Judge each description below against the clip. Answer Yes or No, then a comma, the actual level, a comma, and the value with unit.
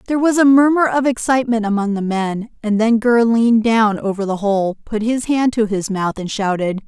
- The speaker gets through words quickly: Yes, fast, 220 wpm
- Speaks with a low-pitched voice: No, high, 225 Hz